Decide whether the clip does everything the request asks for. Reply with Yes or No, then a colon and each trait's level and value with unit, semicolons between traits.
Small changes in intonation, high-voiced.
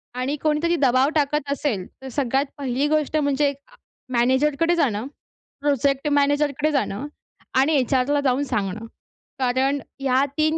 Yes: narrow, 2.3 semitones; very high, 280 Hz